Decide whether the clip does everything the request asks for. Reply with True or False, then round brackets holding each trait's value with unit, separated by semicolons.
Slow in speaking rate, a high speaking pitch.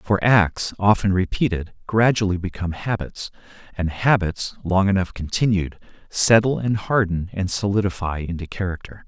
False (125 wpm; 95 Hz)